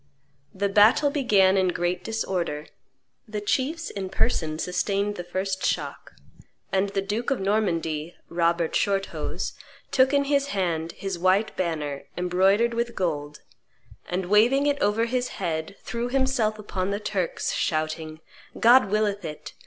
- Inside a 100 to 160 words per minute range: Yes, average, 140 wpm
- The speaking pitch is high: Yes, high, 195 Hz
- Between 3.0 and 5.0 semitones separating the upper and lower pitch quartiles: Yes, average, 4.3 semitones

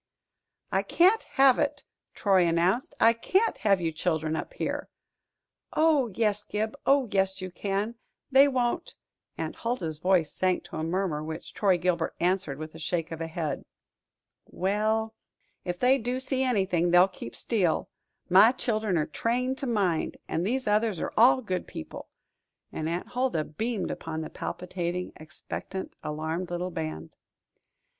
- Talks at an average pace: Yes, average, 155 wpm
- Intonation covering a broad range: Yes, wide, 5.7 semitones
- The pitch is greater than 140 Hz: Yes, high, 190 Hz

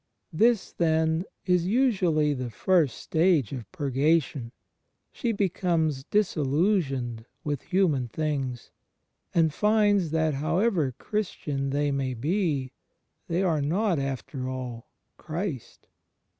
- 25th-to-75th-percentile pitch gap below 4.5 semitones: No, average, 5.3 semitones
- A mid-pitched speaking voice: Yes, medium, 155 Hz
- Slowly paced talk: Yes, slow, 105 wpm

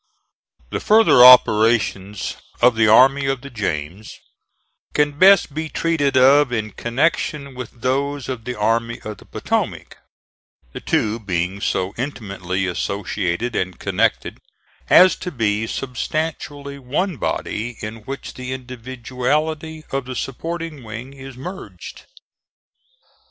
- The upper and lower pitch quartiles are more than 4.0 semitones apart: Yes, average, 4.5 semitones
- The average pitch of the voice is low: Yes, low, 125 Hz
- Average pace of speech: No, slow, 125 wpm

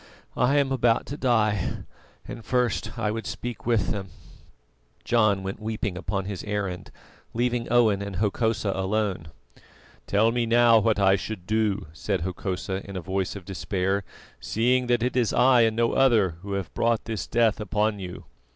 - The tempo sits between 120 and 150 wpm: No, average, 170 wpm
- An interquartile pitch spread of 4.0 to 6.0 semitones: No, average, 3.1 semitones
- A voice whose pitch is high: No, low, 110 Hz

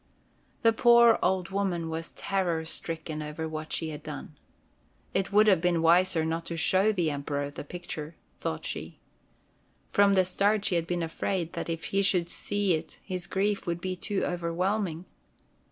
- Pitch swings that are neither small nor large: Yes, average, 3.3 semitones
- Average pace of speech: Yes, average, 170 wpm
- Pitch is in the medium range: Yes, medium, 175 Hz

